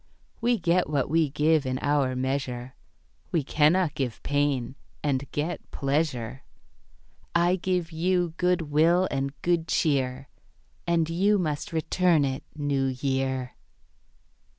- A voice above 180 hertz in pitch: No, medium, 150 Hz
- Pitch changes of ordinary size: Yes, average, 4.2 semitones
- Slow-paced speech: Yes, slow, 125 wpm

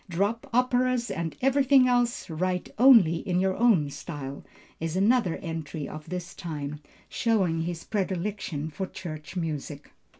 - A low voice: No, medium, 180 Hz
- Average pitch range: No, wide, 6.3 semitones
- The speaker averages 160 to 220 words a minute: No, slow, 135 wpm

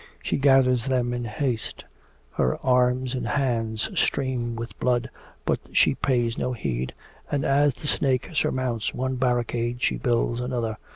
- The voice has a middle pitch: No, low, 125 Hz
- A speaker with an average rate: Yes, average, 150 wpm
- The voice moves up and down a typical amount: No, narrow, 1.8 semitones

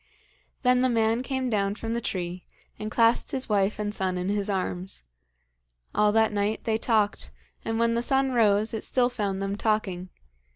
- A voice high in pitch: Yes, high, 215 Hz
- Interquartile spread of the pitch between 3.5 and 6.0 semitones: No, average, 2.8 semitones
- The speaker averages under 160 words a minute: No, average, 180 wpm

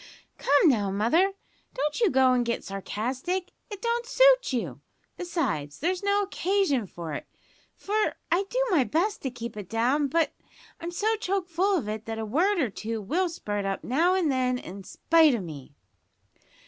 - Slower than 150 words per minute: No, average, 180 wpm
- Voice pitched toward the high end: Yes, very high, 290 Hz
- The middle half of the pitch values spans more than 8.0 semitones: Yes, wide, 8.9 semitones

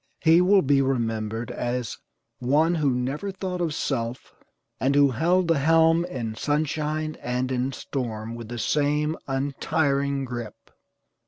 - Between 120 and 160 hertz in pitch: Yes, medium, 140 Hz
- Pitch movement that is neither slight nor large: Yes, average, 4.2 semitones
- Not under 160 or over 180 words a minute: No, average, 140 wpm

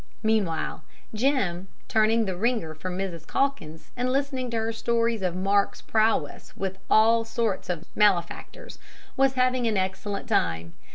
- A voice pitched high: Yes, high, 215 Hz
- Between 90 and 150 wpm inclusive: Yes, average, 145 wpm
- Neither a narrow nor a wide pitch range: Yes, average, 4.1 semitones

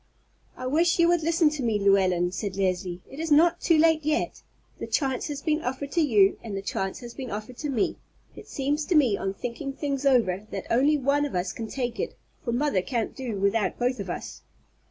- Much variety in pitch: Yes, wide, 6.5 semitones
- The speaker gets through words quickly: Yes, fast, 220 wpm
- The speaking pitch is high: Yes, very high, 255 Hz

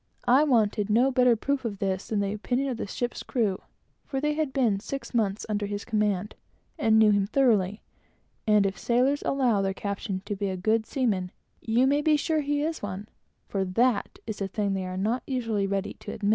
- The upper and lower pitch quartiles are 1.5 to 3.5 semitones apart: No, average, 4.3 semitones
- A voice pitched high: Yes, high, 220 Hz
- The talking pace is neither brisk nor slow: No, fast, 215 wpm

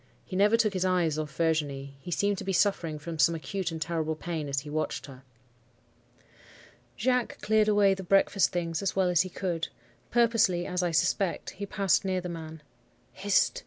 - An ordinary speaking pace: Yes, average, 190 wpm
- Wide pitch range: No, average, 3.6 semitones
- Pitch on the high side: No, medium, 175 Hz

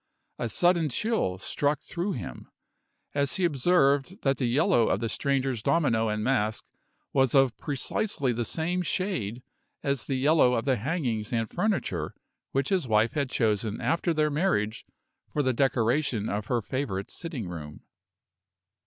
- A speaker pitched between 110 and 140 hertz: Yes, low, 135 Hz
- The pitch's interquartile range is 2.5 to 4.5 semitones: No, wide, 5.6 semitones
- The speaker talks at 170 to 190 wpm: No, average, 155 wpm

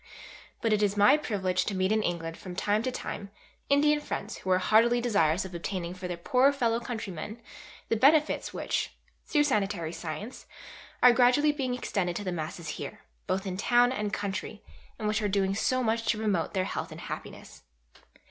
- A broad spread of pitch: No, average, 4.7 semitones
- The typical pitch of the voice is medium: No, high, 210 Hz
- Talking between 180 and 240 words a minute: Yes, average, 185 wpm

